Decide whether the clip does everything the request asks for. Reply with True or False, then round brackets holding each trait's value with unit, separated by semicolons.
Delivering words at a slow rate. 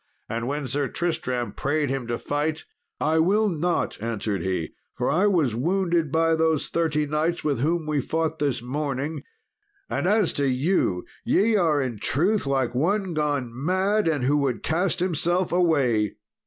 False (165 wpm)